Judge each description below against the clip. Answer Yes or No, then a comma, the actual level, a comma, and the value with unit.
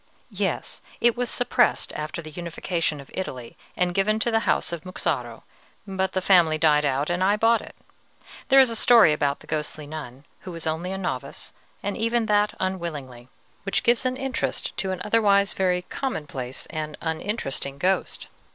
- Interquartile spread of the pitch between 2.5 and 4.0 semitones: No, wide, 5.6 semitones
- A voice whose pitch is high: No, medium, 180 Hz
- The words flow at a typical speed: Yes, average, 175 wpm